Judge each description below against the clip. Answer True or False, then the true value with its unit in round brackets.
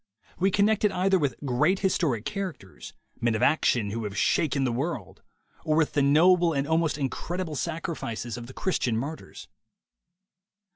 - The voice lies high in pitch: False (150 Hz)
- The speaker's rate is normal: True (155 wpm)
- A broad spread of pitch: True (6.3 semitones)